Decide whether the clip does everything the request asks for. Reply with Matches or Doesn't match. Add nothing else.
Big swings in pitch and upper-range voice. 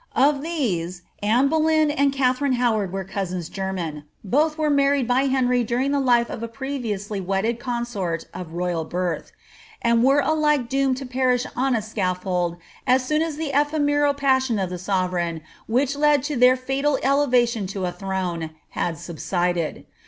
Matches